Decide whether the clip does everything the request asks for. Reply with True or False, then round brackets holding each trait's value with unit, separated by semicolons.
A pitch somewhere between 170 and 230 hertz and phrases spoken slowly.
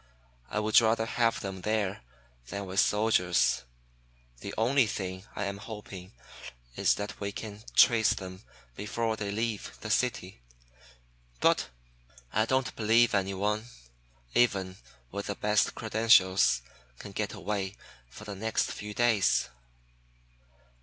False (105 Hz; 125 wpm)